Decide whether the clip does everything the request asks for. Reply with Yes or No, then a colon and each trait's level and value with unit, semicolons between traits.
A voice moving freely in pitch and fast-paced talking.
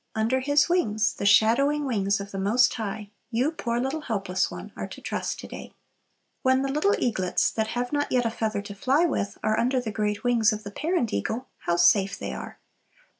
No: average, 4.4 semitones; fast, 210 wpm